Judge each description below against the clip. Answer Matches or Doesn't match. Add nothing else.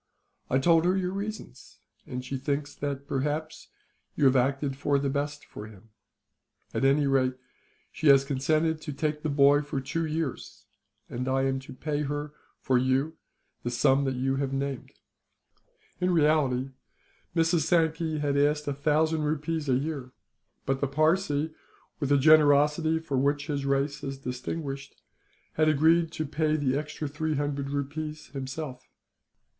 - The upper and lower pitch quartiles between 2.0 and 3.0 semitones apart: Matches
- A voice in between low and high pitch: Matches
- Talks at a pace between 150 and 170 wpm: Matches